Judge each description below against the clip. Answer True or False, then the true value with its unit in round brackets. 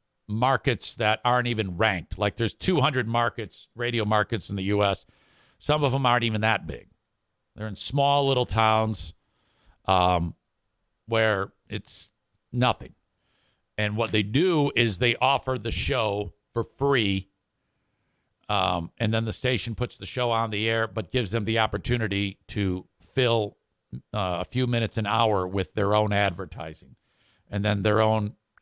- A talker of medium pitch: False (110 Hz)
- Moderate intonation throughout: True (3.0 semitones)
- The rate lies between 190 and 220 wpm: False (155 wpm)